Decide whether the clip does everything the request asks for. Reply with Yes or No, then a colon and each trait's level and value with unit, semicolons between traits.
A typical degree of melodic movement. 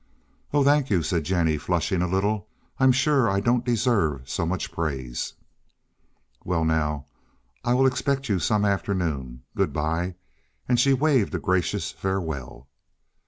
No: wide, 7.3 semitones